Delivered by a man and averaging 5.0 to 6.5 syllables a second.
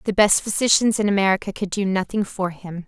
No: female; 5.9 syllables/s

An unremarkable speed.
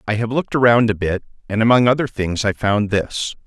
No: fast, 225 wpm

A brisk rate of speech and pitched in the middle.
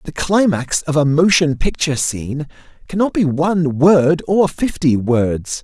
No: average, 150 wpm; medium, 155 Hz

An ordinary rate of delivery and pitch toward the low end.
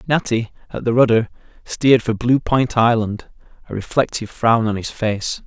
Yes: average, 165 wpm; low, 115 Hz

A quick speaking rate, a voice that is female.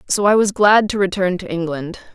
Yes: fast, 225 wpm; female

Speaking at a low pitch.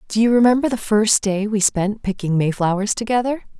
No: high, 215 Hz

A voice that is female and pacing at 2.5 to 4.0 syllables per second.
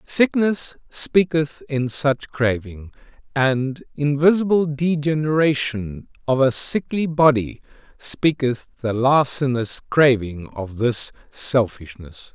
No: male; 3.5 syllables/s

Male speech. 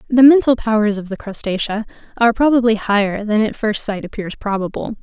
No: female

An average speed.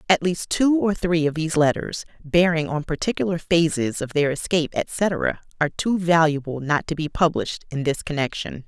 Yes: average, 180 wpm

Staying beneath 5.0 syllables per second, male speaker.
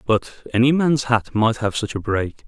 Yes: 4.4 syllables/s; male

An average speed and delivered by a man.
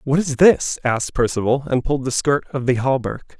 No: fast, 210 wpm; male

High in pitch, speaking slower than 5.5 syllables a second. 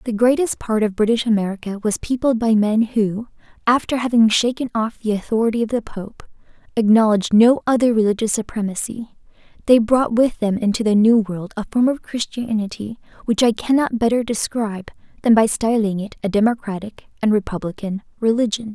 No: high, 220 Hz; 5.6 syllables/s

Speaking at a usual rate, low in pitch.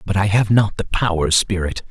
No: fast, 220 wpm; very low, 95 Hz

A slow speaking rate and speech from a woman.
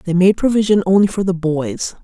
No: fast, 205 wpm; female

